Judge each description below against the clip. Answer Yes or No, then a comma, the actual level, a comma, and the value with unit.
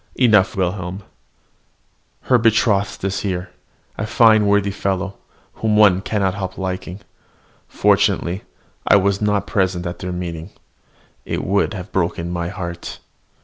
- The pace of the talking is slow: Yes, slow, 130 wpm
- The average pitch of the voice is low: Yes, very low, 95 Hz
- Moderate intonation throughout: No, narrow, 2.2 semitones